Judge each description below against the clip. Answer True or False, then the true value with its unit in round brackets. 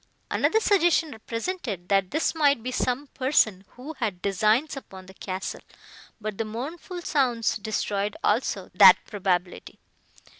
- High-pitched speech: True (230 Hz)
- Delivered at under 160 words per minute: True (135 wpm)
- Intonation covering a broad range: True (6.6 semitones)